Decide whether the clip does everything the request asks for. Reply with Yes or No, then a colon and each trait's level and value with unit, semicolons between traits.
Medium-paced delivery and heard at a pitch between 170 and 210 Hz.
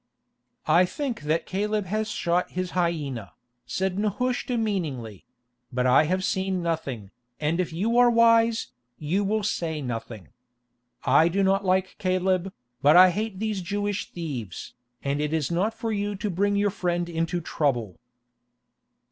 Yes: average, 150 wpm; medium, 185 Hz